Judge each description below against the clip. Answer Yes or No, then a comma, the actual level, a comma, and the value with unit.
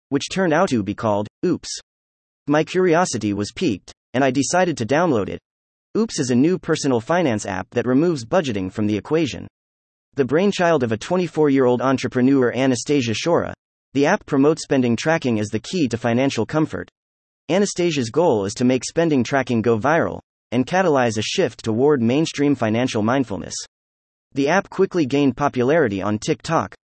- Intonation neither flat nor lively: No, wide, 6.0 semitones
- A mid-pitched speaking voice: No, low, 130 Hz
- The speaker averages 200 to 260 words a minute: No, average, 170 wpm